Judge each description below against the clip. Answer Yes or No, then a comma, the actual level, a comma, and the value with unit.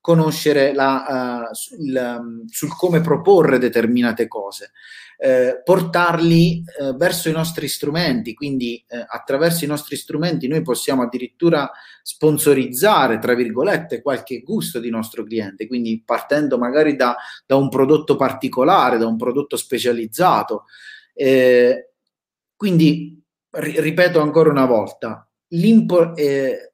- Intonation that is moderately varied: Yes, average, 4.8 semitones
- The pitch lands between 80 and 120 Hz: No, medium, 140 Hz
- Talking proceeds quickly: No, average, 120 wpm